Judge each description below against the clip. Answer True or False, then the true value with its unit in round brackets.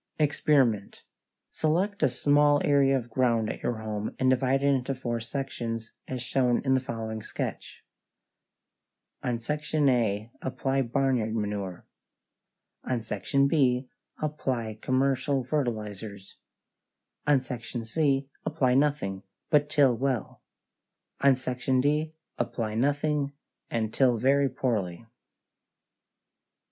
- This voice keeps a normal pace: False (115 wpm)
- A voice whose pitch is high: False (130 Hz)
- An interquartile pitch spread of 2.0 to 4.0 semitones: True (3.5 semitones)